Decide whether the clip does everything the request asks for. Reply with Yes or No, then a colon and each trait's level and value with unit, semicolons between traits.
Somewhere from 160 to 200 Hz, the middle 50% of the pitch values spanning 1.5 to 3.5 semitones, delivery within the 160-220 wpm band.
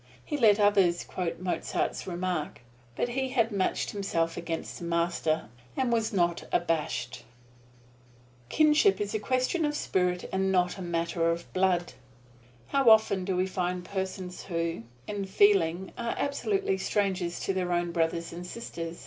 No: medium, 185 Hz; average, 3.2 semitones; average, 150 wpm